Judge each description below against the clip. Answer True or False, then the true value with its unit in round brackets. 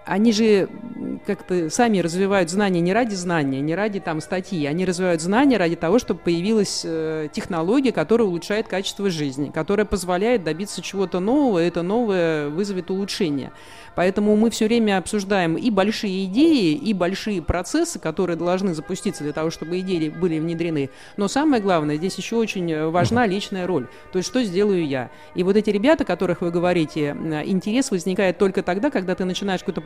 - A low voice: False (190 Hz)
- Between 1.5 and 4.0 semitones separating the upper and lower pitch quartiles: True (3.7 semitones)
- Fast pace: True (170 wpm)